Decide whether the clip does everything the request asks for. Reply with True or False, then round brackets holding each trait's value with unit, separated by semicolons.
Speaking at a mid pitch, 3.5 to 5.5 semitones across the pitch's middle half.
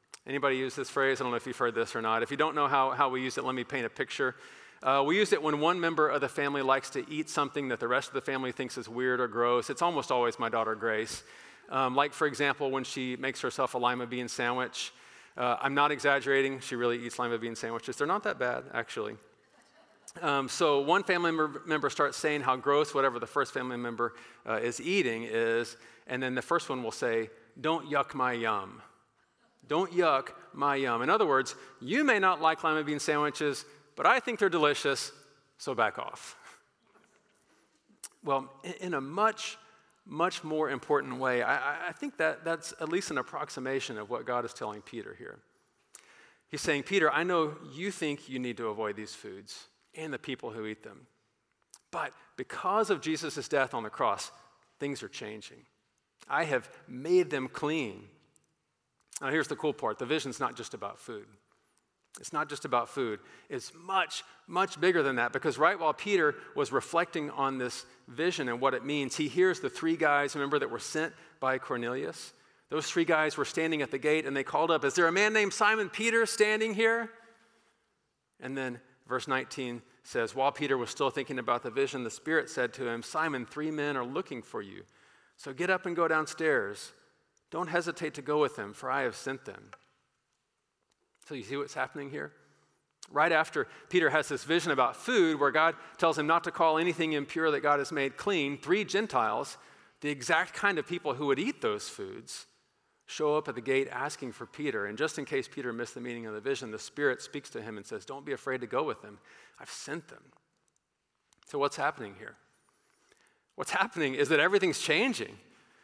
True (145 Hz; 4.3 semitones)